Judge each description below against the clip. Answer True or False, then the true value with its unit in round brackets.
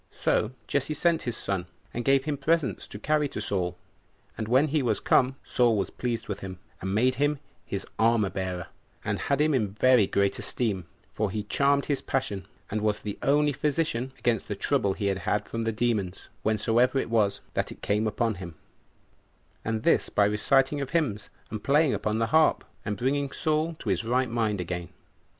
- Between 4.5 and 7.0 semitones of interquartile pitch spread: True (5.0 semitones)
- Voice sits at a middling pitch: False (115 Hz)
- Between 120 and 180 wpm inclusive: False (190 wpm)